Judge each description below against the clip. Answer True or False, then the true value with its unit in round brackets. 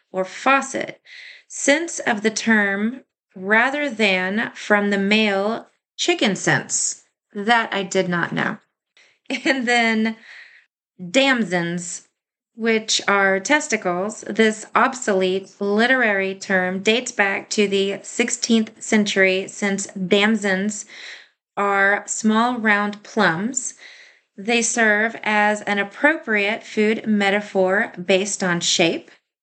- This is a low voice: False (210 Hz)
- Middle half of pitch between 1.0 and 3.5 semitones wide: True (3.0 semitones)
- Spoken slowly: True (100 wpm)